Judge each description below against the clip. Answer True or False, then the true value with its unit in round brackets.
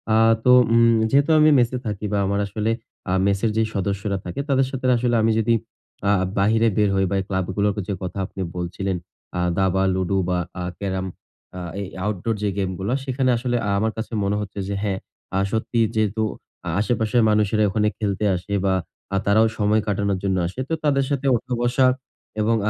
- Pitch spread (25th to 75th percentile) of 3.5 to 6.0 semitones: False (3.0 semitones)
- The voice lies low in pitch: True (105 Hz)